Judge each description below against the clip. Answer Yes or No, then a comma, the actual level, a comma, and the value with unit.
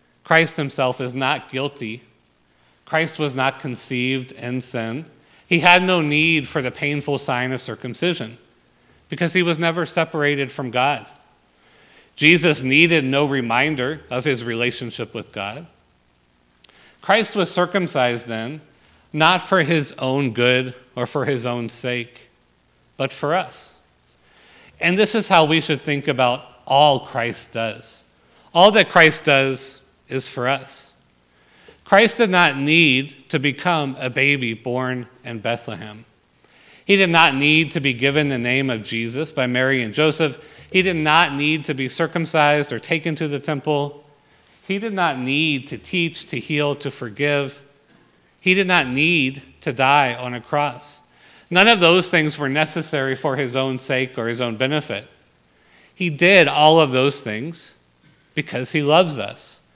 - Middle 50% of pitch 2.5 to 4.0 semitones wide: No, average, 4.4 semitones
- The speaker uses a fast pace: No, average, 155 wpm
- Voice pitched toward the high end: No, medium, 140 Hz